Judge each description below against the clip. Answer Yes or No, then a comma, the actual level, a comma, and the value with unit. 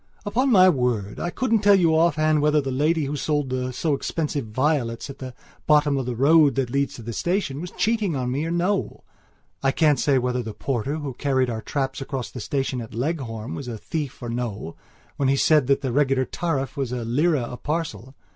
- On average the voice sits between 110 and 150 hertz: Yes, medium, 140 Hz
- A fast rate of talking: Yes, fast, 210 wpm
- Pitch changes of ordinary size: Yes, average, 3.8 semitones